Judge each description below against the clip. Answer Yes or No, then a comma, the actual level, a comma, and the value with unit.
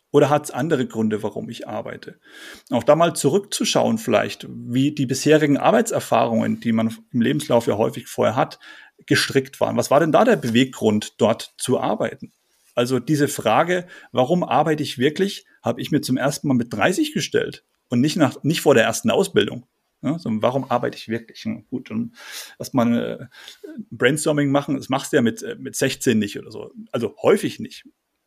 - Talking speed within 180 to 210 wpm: Yes, average, 185 wpm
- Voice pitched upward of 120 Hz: Yes, medium, 140 Hz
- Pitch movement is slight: No, average, 4.3 semitones